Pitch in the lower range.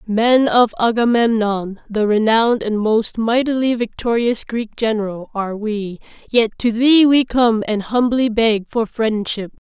No: high, 225 Hz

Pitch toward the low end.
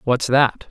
Yes: low, 130 Hz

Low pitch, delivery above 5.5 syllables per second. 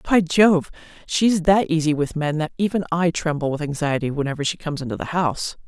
No: medium, 160 Hz; 5.9 syllables/s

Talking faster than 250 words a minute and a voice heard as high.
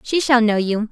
Yes: fast, 265 wpm; high, 230 Hz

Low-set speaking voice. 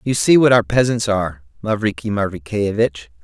Yes: low, 105 Hz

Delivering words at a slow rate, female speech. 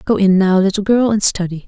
No: fast, 250 wpm; female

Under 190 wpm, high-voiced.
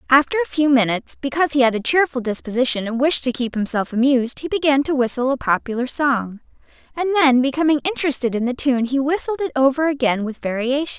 No: average, 200 wpm; very high, 265 Hz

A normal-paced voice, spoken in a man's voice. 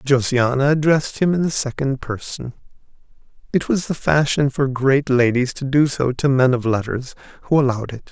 Yes: average, 175 wpm; male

